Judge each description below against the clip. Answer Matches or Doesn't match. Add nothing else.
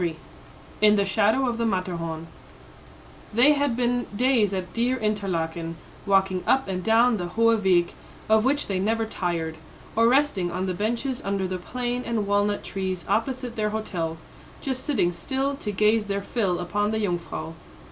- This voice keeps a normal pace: Matches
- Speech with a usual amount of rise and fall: Matches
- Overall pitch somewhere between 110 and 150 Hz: Doesn't match